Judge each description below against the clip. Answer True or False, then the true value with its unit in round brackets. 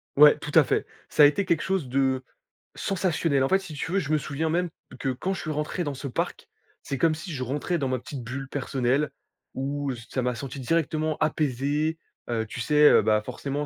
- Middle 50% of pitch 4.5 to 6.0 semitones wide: False (3.2 semitones)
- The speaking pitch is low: False (145 Hz)